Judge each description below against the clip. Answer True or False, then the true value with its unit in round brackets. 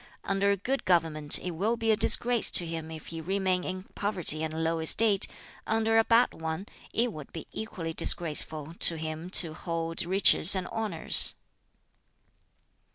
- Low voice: False (180 Hz)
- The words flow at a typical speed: True (160 wpm)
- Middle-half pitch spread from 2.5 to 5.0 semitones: True (4.3 semitones)